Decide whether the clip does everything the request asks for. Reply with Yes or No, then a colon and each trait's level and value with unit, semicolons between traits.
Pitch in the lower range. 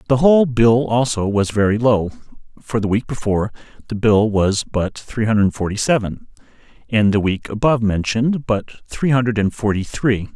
Yes: low, 110 Hz